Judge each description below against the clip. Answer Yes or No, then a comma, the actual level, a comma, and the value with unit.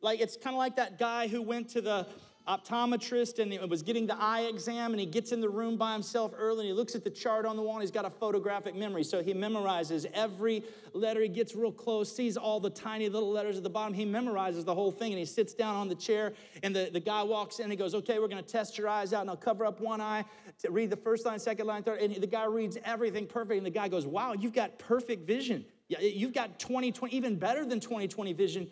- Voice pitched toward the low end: No, high, 220 Hz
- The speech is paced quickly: Yes, fast, 265 wpm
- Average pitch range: No, narrow, 2.0 semitones